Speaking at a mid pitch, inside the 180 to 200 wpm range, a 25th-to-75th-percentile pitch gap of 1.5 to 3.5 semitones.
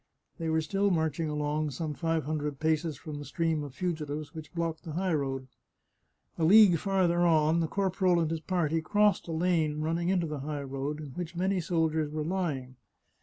Yes: medium, 160 Hz; average, 190 wpm; narrow, 2.5 semitones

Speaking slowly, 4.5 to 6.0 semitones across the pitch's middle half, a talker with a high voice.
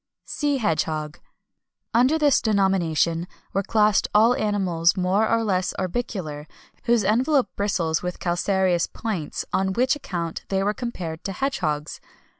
Yes: slow, 130 wpm; average, 5.0 semitones; high, 195 Hz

